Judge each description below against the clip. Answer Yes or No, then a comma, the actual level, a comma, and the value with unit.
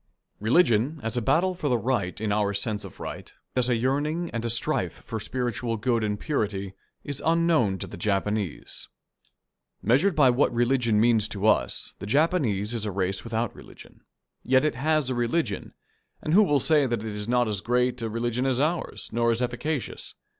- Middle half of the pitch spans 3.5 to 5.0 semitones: Yes, average, 4.3 semitones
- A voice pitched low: Yes, low, 120 Hz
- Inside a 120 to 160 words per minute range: No, average, 190 wpm